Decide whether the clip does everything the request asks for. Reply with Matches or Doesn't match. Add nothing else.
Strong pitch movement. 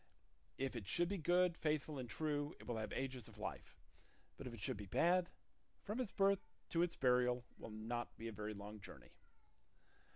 Matches